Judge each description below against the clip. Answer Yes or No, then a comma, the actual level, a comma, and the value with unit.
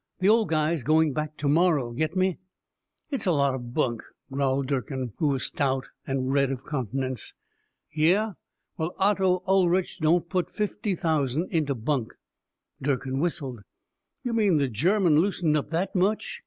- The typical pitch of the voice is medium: Yes, medium, 155 Hz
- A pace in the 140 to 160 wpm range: Yes, average, 155 wpm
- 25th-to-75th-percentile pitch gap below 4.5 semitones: No, average, 5.2 semitones